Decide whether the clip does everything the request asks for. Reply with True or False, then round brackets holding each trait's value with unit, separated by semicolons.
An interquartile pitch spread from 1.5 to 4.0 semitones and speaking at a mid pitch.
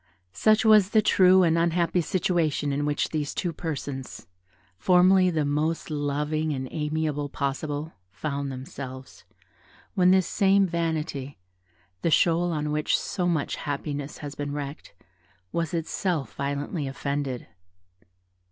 True (3.3 semitones; 155 Hz)